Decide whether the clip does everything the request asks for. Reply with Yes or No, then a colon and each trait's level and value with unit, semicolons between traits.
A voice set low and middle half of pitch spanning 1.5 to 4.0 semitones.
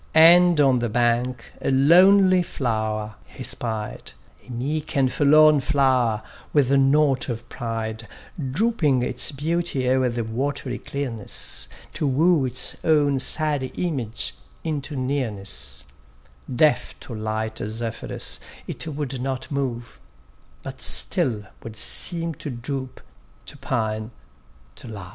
No: low, 130 Hz; average, 4.5 semitones